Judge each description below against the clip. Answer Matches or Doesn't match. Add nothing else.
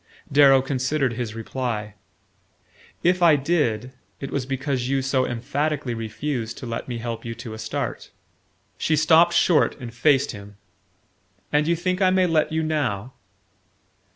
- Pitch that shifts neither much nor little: Matches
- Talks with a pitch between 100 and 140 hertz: Matches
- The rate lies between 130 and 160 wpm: Matches